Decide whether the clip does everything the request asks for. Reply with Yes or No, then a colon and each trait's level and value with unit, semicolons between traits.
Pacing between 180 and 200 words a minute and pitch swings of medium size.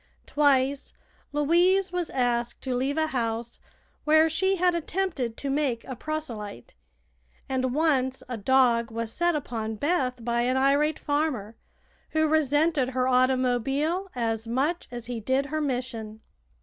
No: average, 140 wpm; average, 4.4 semitones